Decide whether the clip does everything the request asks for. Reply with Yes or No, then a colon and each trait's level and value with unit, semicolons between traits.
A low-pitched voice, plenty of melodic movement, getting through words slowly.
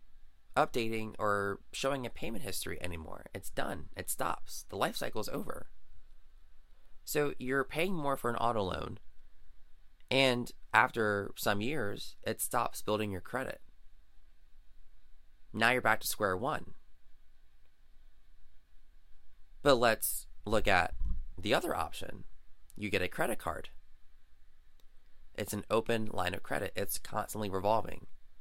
Yes: very low, 85 Hz; wide, 8.1 semitones; slow, 125 wpm